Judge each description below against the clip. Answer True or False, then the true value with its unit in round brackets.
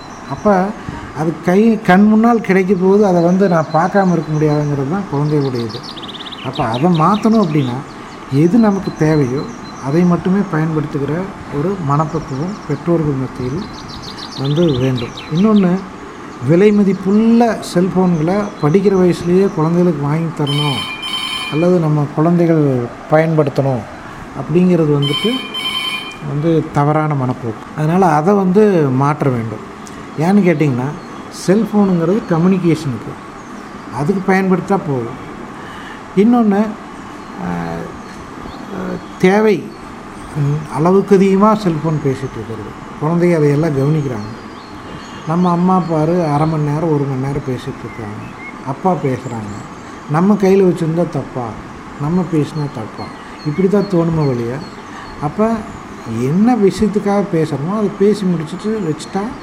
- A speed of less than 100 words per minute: False (105 wpm)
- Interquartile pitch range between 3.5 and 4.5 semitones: False (5.1 semitones)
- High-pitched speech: False (160 Hz)